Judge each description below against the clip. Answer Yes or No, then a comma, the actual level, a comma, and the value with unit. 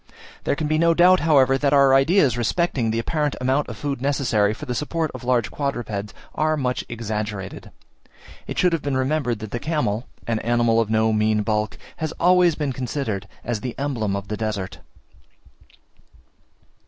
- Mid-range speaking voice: No, low, 125 Hz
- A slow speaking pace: No, average, 175 wpm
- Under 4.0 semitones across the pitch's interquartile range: No, average, 5.2 semitones